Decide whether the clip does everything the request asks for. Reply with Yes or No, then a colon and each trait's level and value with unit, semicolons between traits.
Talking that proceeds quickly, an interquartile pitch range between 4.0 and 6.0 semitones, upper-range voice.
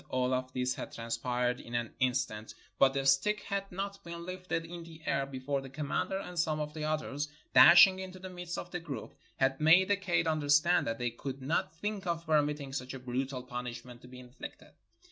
No: fast, 215 wpm; average, 5.2 semitones; medium, 145 Hz